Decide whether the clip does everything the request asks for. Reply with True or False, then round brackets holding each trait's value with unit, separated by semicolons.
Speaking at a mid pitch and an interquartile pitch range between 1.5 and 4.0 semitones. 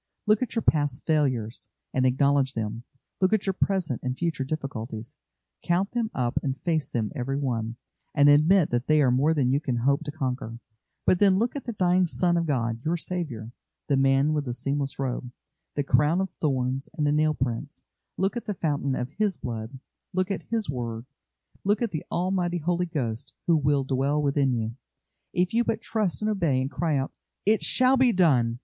False (145 Hz; 5.6 semitones)